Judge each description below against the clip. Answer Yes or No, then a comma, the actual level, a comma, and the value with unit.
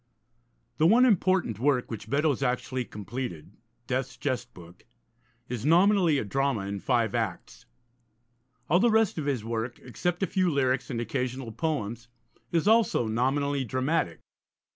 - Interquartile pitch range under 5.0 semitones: No, wide, 5.5 semitones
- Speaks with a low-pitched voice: Yes, low, 130 Hz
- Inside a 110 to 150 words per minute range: Yes, average, 140 wpm